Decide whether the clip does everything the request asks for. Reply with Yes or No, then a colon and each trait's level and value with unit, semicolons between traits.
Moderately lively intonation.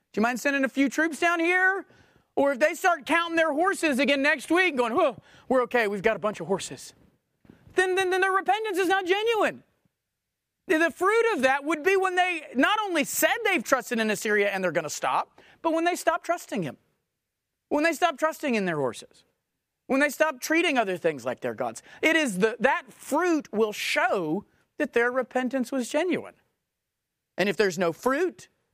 No: wide, 6.3 semitones